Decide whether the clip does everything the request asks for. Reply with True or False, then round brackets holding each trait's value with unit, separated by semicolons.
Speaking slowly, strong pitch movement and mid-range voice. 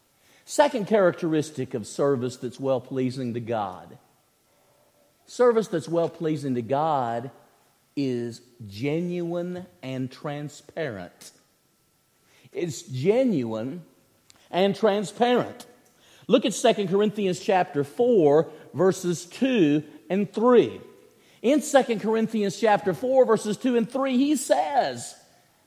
True (105 wpm; 8.8 semitones; 175 Hz)